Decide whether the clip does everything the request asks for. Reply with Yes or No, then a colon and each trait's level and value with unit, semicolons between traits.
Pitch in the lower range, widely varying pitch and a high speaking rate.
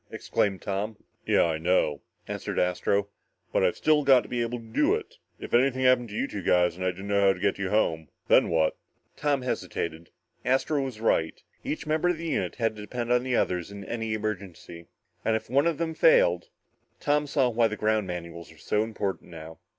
Yes: low, 110 Hz; wide, 6.1 semitones; fast, 210 wpm